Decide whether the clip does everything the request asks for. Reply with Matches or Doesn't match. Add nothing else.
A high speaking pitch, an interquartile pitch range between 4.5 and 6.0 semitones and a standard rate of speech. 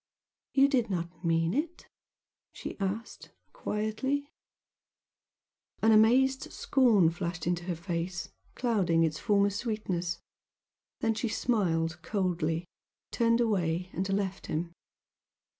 Doesn't match